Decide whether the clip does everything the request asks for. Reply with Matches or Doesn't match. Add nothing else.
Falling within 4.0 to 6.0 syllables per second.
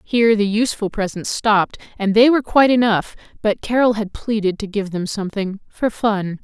Matches